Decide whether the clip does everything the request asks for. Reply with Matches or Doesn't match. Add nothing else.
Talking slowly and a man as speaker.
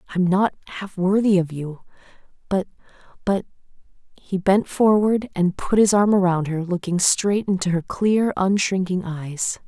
Doesn't match